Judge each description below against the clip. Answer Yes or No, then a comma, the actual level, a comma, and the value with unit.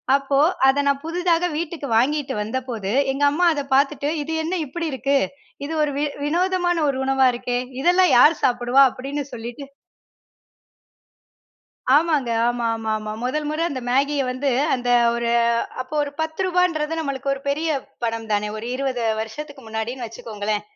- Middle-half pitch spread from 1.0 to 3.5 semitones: No, average, 4.0 semitones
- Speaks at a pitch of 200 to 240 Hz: No, very high, 275 Hz